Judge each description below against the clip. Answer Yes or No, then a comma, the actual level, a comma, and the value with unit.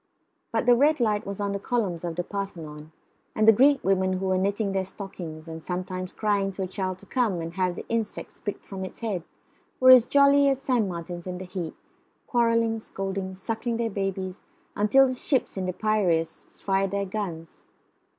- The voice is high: Yes, high, 195 Hz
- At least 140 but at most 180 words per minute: No, average, 195 wpm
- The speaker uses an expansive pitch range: No, average, 3.5 semitones